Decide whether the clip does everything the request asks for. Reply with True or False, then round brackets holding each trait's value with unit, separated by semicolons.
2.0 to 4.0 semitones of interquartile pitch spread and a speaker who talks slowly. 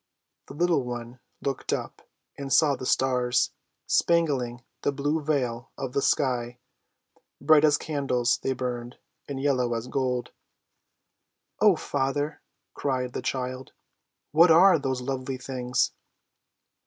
True (2.4 semitones; 125 wpm)